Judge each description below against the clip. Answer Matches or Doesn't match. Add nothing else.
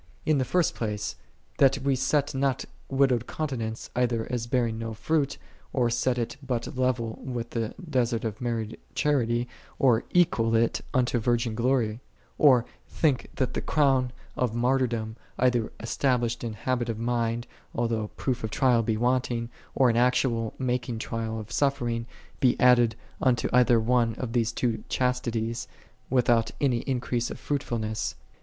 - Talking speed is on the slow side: Doesn't match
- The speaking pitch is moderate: Doesn't match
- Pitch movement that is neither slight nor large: Doesn't match